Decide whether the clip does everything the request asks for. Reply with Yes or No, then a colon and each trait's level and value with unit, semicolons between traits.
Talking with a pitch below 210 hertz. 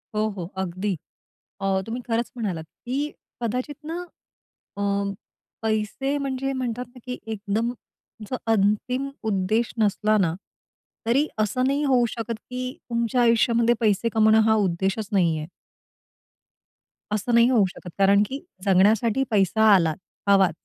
No: high, 220 Hz